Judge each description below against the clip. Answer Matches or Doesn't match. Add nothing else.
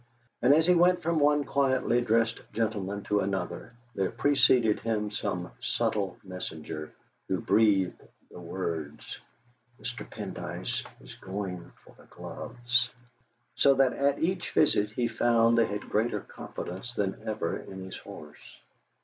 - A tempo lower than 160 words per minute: Matches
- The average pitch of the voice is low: Matches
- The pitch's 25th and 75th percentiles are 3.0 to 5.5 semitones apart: Matches